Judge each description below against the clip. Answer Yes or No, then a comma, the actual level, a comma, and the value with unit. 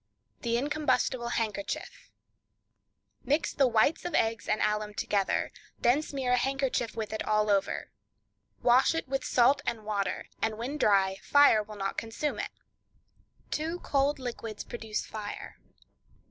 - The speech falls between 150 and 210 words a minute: No, slow, 135 wpm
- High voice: Yes, high, 235 Hz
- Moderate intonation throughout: Yes, average, 4.3 semitones